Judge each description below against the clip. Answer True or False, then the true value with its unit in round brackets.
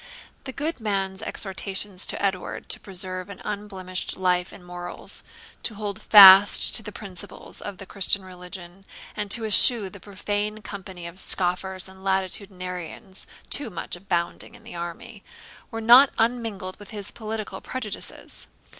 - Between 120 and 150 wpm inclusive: True (145 wpm)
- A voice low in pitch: False (195 Hz)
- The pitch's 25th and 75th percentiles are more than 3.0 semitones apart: False (2.4 semitones)